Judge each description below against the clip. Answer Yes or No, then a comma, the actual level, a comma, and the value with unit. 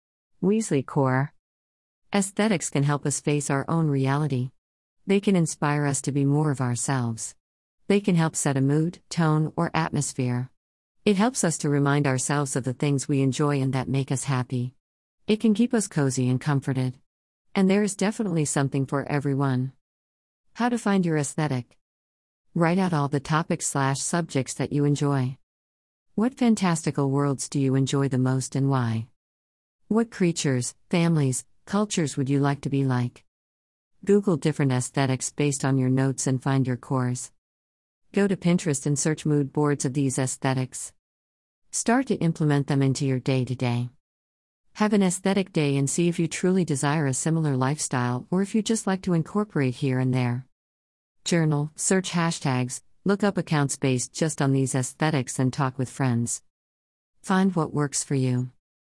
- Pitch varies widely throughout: No, average, 4.3 semitones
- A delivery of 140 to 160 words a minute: No, average, 170 wpm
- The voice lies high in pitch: No, medium, 140 Hz